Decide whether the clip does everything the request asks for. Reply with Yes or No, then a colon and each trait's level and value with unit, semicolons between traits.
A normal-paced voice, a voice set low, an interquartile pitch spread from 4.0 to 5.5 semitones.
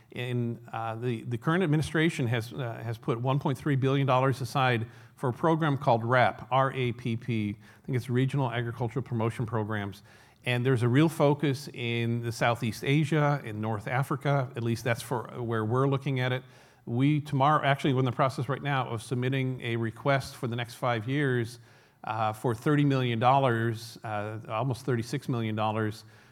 No: average, 180 wpm; low, 125 Hz; average, 2.9 semitones